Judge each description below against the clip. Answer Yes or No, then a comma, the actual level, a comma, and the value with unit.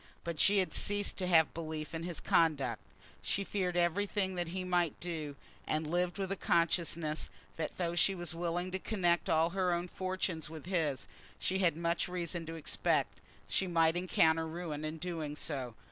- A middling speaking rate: Yes, average, 185 wpm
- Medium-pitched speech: Yes, medium, 170 Hz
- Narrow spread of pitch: Yes, narrow, 2.2 semitones